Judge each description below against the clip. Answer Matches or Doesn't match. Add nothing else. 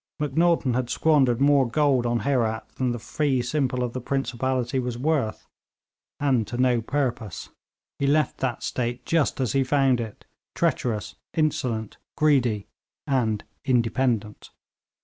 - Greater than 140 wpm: Doesn't match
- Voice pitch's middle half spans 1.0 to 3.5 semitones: Matches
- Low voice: Matches